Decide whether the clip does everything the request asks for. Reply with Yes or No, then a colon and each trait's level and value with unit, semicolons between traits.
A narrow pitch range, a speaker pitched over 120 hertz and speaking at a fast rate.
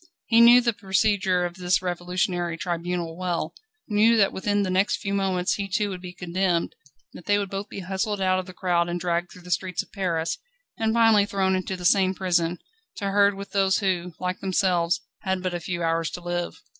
Yes: narrow, 2.1 semitones; medium, 185 Hz; fast, 210 wpm